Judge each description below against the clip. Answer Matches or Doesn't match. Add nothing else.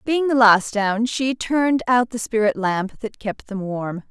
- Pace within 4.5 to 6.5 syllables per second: Doesn't match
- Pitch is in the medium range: Doesn't match